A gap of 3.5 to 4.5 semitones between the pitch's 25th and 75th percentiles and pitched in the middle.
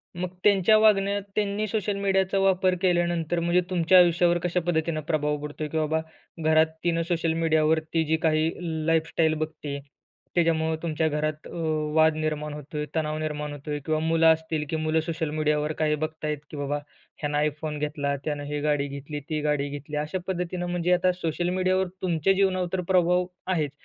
No: average, 2.7 semitones; medium, 160 Hz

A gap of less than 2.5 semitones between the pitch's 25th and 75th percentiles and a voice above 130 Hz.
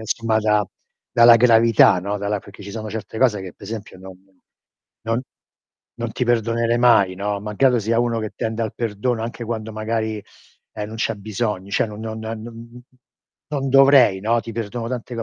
No: narrow, 1.9 semitones; low, 110 Hz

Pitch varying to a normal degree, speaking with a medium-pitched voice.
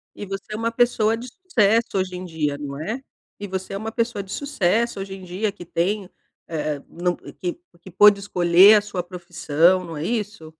No: average, 3.7 semitones; high, 195 Hz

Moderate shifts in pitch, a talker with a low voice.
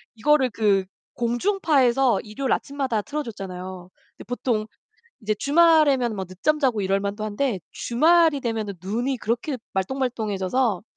No: average, 5.0 semitones; high, 235 Hz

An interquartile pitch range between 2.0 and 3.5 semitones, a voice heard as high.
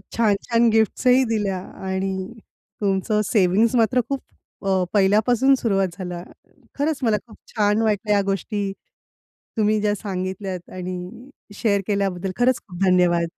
Yes: average, 2.9 semitones; high, 205 Hz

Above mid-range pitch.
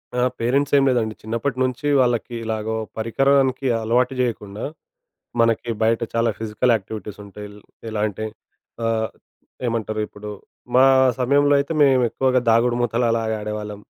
No: low, 115 Hz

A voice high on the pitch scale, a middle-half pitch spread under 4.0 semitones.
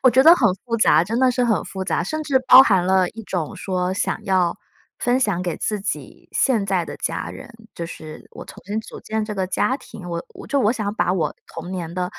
No: high, 200 Hz; average, 4.4 semitones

